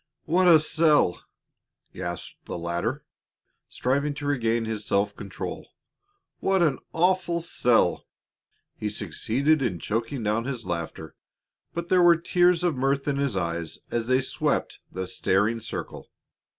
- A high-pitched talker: No, low, 125 Hz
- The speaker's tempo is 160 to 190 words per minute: No, slow, 135 wpm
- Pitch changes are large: Yes, wide, 7.4 semitones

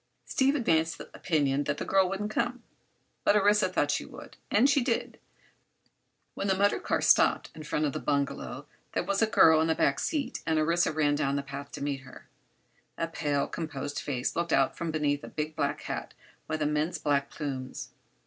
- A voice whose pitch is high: No, medium, 155 Hz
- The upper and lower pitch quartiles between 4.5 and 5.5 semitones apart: Yes, average, 5.1 semitones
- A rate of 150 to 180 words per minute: No, average, 195 wpm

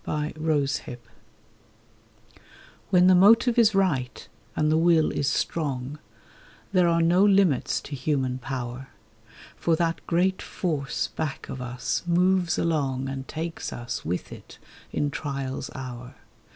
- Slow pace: Yes, slow, 125 wpm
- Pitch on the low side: No, medium, 155 Hz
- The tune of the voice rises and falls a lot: No, average, 4.7 semitones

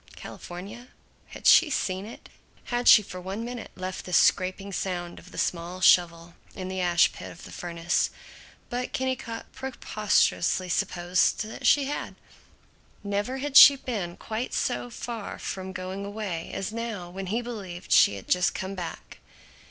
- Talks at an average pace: Yes, average, 160 wpm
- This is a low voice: No, high, 195 Hz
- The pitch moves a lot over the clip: No, average, 4.5 semitones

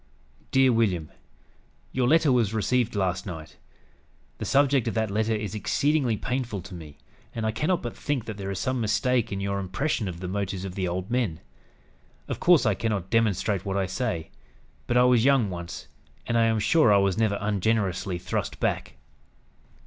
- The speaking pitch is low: Yes, low, 110 Hz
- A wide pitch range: No, average, 4.4 semitones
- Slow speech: No, average, 185 wpm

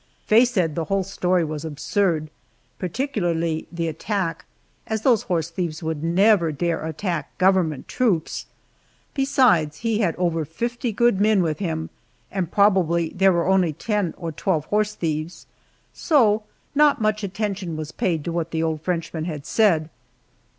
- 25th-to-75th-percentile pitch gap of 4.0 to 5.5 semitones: Yes, average, 4.4 semitones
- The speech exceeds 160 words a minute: No, average, 150 wpm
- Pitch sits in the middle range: Yes, medium, 175 Hz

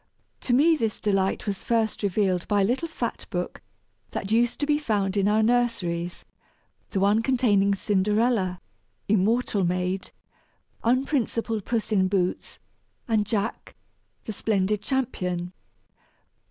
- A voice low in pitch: No, high, 210 Hz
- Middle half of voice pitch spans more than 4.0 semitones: No, average, 3.4 semitones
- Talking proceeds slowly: Yes, slow, 125 wpm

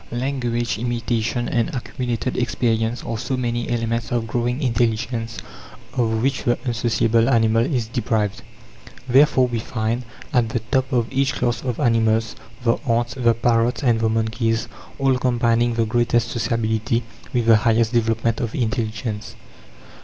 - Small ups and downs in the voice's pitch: Yes, narrow, 1.3 semitones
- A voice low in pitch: Yes, low, 115 Hz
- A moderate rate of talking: Yes, average, 145 wpm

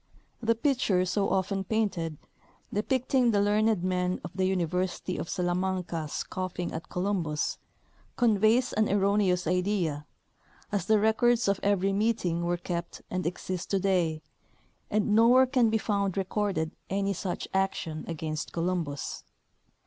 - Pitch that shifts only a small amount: No, average, 3.1 semitones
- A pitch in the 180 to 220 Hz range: Yes, high, 190 Hz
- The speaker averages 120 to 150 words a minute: Yes, average, 140 wpm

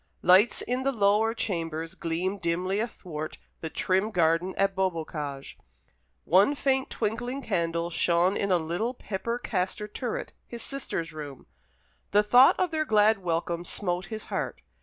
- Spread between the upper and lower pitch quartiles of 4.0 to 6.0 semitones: Yes, average, 5.0 semitones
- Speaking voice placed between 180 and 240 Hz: Yes, high, 190 Hz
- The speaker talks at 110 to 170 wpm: Yes, average, 145 wpm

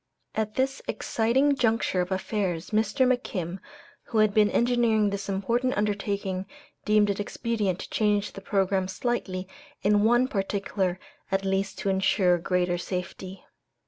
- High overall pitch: Yes, high, 205 Hz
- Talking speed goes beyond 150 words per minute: No, average, 140 wpm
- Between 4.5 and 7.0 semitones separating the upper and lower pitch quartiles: No, average, 2.7 semitones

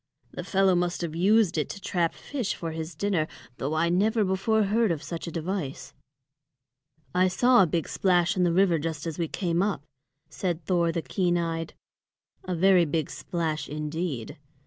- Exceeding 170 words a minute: Yes, average, 180 wpm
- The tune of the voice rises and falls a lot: No, average, 2.7 semitones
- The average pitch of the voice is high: No, medium, 175 Hz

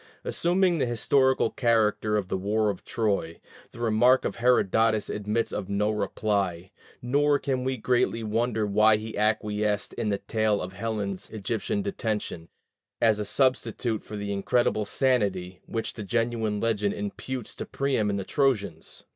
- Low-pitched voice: Yes, low, 110 Hz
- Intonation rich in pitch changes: No, average, 2.9 semitones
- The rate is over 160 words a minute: No, average, 155 wpm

